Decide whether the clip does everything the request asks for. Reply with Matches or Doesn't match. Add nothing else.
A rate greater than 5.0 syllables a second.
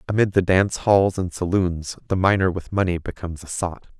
Matches